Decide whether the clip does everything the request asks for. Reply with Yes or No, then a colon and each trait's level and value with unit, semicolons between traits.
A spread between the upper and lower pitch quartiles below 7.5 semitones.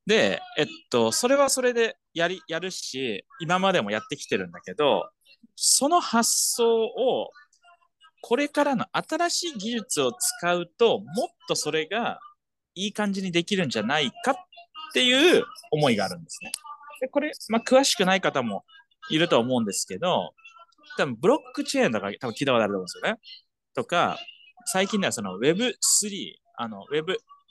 No: wide, 9.0 semitones